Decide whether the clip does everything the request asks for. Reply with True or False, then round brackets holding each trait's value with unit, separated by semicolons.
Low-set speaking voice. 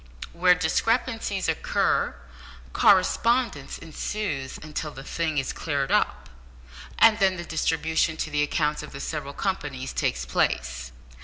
False (160 Hz)